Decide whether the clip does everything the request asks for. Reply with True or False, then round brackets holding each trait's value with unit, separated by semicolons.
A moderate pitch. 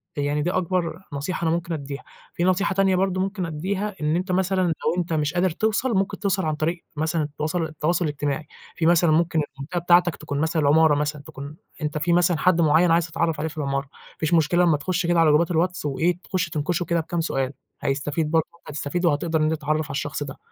True (160 Hz)